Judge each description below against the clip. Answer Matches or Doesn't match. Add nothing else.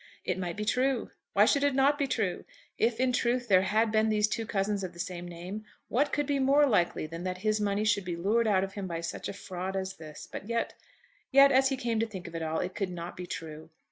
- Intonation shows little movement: Doesn't match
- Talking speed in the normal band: Doesn't match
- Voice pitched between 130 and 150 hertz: Doesn't match